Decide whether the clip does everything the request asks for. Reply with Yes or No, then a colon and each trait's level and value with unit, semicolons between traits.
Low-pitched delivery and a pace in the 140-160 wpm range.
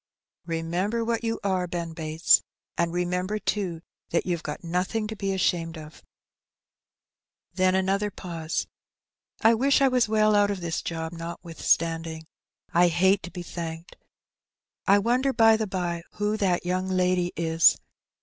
No: medium, 180 Hz; average, 155 wpm